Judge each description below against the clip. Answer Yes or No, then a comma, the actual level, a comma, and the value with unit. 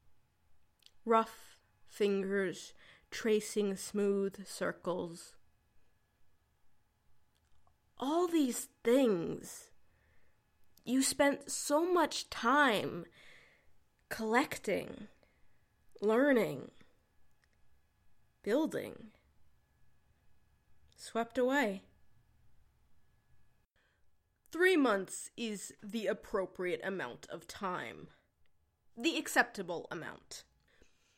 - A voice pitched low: No, high, 205 Hz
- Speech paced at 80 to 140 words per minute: No, slow, 55 wpm